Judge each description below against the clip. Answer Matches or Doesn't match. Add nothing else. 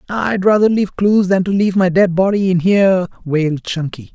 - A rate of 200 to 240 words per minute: Matches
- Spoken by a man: Matches